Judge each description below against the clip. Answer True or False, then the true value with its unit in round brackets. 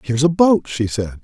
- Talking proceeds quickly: True (245 wpm)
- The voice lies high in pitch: False (140 Hz)